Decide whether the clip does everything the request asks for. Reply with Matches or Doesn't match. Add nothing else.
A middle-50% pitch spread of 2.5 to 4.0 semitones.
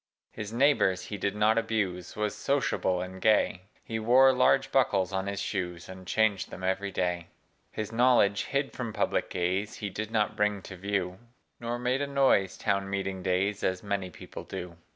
Matches